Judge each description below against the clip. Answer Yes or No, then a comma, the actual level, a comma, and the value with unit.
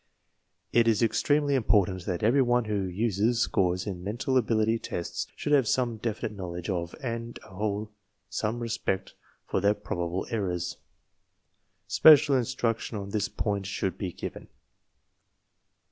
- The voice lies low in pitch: Yes, low, 105 Hz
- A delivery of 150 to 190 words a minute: No, average, 140 wpm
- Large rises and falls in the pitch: No, average, 3.7 semitones